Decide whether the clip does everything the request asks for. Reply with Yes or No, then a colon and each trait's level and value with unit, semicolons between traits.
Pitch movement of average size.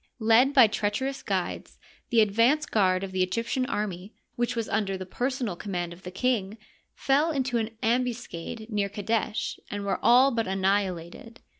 Yes: average, 4.2 semitones